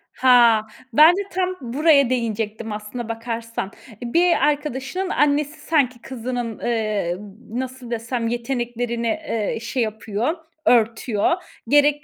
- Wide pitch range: No, average, 4.1 semitones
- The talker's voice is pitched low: No, high, 240 Hz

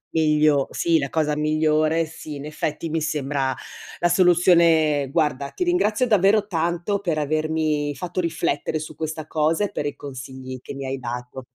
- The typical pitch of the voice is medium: Yes, medium, 155 Hz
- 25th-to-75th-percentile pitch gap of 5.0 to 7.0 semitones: No, narrow, 2.5 semitones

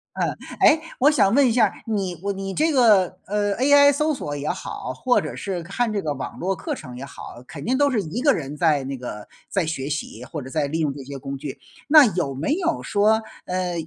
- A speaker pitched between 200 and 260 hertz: No, high, 190 Hz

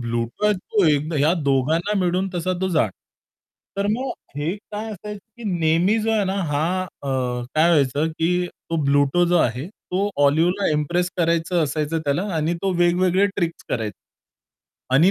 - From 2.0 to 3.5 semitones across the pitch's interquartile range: No, average, 4.1 semitones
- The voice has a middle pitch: Yes, medium, 170 Hz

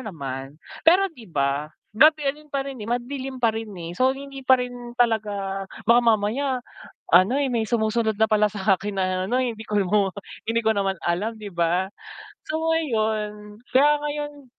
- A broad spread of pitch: No, average, 4.4 semitones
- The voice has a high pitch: Yes, high, 225 Hz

